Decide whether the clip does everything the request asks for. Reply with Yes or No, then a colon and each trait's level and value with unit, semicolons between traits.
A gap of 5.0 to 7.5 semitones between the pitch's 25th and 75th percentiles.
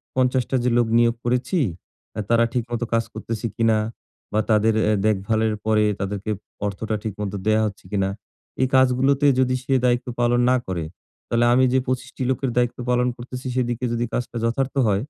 No: average, 2.7 semitones